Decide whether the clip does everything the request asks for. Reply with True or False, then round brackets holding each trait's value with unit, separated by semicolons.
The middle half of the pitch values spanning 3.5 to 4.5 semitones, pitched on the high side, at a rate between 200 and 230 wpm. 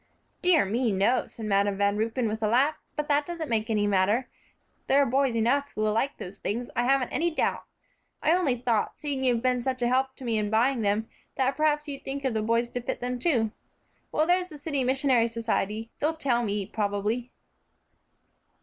True (4.0 semitones; 245 Hz; 205 wpm)